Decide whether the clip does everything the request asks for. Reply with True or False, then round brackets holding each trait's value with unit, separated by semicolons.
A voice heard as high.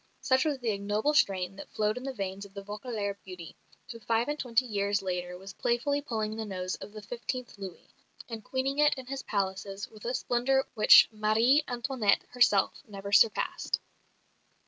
True (215 Hz)